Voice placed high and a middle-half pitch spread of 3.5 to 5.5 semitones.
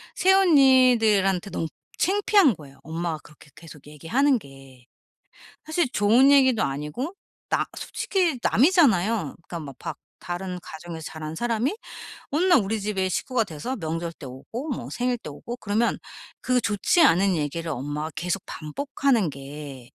No: high, 195 Hz; wide, 8.6 semitones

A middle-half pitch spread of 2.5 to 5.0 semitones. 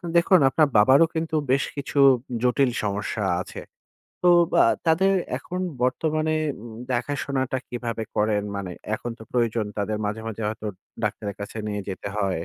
No: wide, 5.4 semitones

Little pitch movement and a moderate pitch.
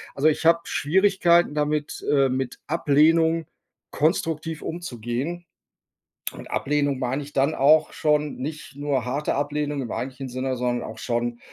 No: average, 3.0 semitones; medium, 145 Hz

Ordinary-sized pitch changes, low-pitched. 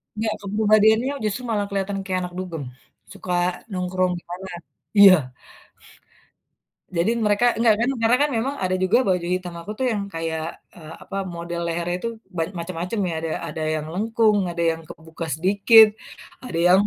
No: average, 3.9 semitones; medium, 185 Hz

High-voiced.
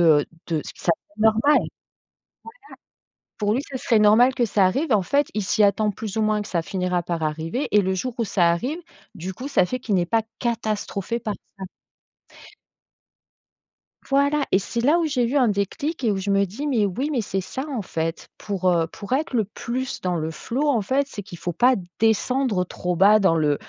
Yes: high, 210 Hz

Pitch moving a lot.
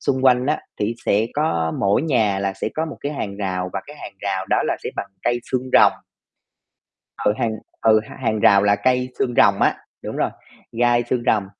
No: average, 4.3 semitones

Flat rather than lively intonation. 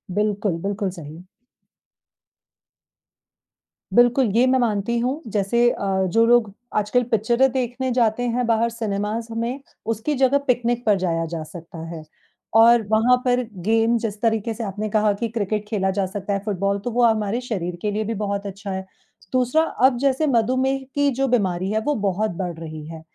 No: average, 3.5 semitones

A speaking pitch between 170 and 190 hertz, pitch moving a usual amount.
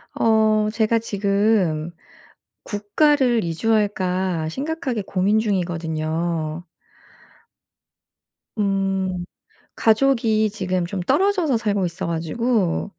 No: high, 200 Hz; average, 4.2 semitones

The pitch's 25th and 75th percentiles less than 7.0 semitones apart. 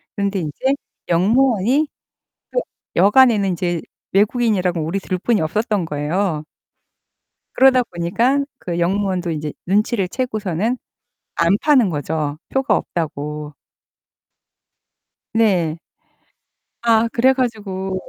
Yes: wide, 5.4 semitones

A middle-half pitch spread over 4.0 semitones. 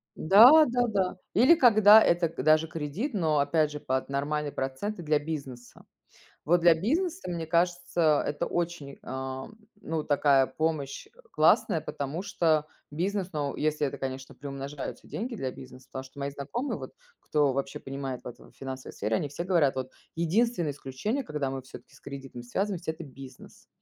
Yes: average, 4.9 semitones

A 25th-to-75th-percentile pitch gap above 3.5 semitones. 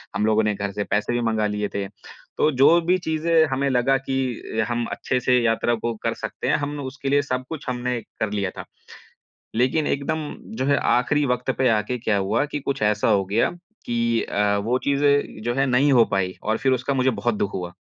Yes: average, 4.4 semitones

